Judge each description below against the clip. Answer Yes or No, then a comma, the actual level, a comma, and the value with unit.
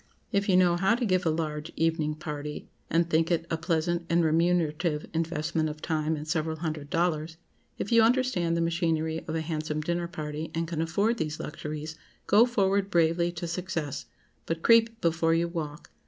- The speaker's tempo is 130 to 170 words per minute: No, average, 180 wpm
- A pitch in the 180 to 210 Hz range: No, medium, 165 Hz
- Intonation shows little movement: Yes, narrow, 1.9 semitones